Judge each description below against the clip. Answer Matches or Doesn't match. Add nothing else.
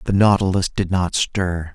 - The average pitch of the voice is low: Matches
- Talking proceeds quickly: Doesn't match